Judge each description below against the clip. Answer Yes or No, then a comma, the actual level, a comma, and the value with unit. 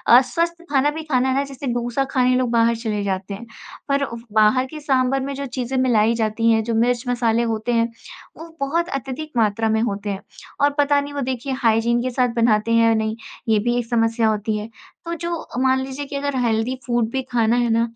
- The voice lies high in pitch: Yes, high, 240 Hz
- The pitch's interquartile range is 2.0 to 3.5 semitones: Yes, average, 3.1 semitones